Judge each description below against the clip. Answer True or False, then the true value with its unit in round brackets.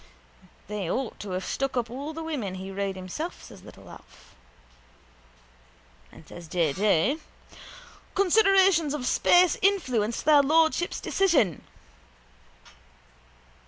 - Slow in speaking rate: True (115 wpm)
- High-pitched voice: True (260 Hz)